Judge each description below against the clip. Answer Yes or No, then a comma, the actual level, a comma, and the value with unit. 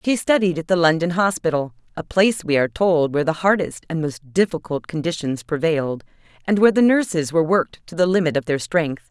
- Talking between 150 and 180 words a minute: No, average, 200 wpm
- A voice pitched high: No, medium, 165 Hz